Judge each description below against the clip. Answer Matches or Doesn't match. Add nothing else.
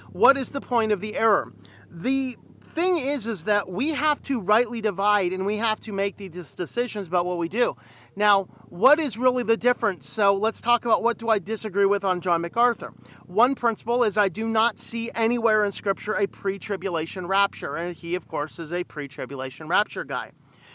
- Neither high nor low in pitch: Doesn't match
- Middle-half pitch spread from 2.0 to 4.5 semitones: Matches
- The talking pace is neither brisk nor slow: Matches